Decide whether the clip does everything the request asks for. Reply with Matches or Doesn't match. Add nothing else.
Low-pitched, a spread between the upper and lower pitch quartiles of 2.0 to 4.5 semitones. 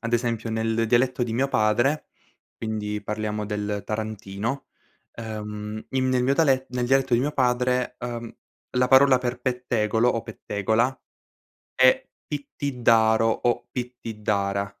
Matches